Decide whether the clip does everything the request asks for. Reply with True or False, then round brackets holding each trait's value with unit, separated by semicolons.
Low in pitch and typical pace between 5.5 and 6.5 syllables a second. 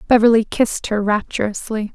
False (220 Hz; 5.6 syllables/s)